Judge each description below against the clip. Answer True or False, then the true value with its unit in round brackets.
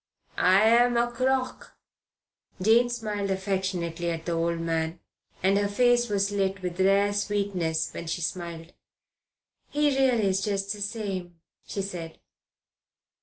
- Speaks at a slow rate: True (130 wpm)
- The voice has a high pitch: True (195 Hz)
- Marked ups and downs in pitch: False (3.9 semitones)